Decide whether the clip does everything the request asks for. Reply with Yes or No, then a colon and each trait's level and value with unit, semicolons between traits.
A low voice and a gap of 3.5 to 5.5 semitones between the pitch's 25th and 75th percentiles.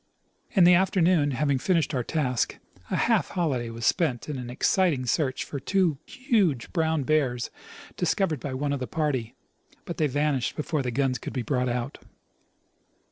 No: medium, 145 Hz; average, 4.8 semitones